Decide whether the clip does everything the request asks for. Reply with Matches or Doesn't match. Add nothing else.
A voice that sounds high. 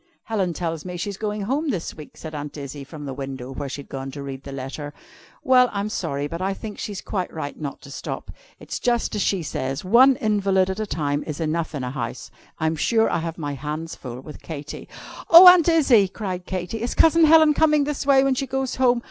Doesn't match